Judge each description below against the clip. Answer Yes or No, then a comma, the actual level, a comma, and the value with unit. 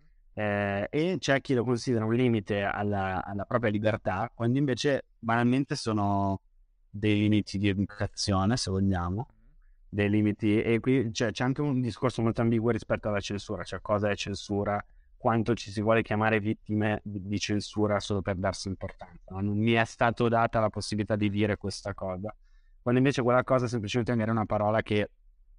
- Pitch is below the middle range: Yes, low, 105 Hz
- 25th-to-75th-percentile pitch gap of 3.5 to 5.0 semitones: No, narrow, 2.6 semitones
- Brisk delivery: Yes, fast, 175 wpm